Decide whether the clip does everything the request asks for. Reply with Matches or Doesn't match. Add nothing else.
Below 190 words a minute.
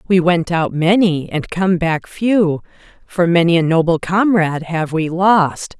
Matches